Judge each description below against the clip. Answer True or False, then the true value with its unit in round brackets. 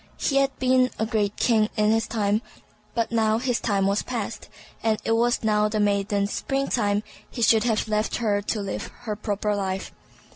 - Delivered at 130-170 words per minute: False (195 wpm)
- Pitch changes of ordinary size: False (2.1 semitones)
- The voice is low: False (215 Hz)